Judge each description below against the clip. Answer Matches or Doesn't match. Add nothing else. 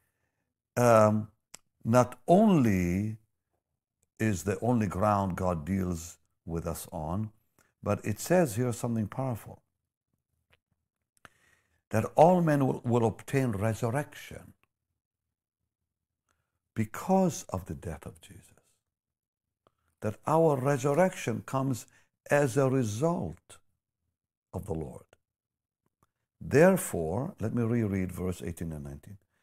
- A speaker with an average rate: Doesn't match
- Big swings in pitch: Doesn't match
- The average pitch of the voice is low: Matches